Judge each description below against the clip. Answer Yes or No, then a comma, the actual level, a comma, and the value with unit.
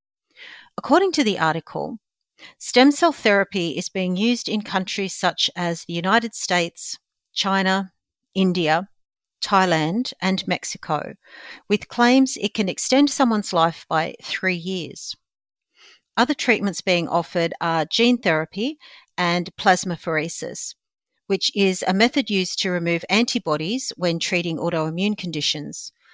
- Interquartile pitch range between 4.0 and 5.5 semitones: Yes, average, 5.2 semitones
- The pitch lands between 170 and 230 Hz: Yes, high, 190 Hz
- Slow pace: Yes, slow, 120 wpm